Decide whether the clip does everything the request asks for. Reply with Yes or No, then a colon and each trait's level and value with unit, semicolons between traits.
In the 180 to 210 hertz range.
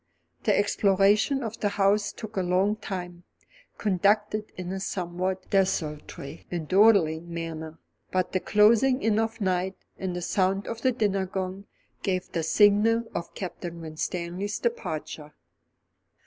Yes: high, 190 Hz